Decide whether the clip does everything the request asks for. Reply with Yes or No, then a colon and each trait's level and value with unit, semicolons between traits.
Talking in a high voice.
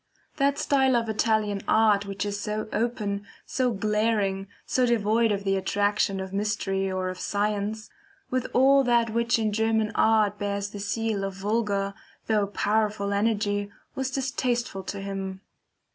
Yes: high, 210 Hz